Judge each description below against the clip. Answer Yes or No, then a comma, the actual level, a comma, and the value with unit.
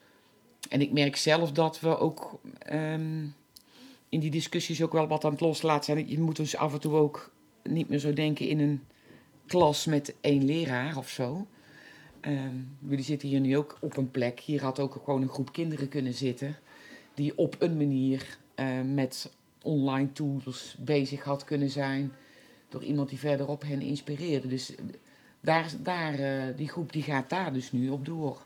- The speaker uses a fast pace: No, average, 180 wpm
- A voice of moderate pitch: Yes, medium, 145 Hz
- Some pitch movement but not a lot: No, narrow, 2.0 semitones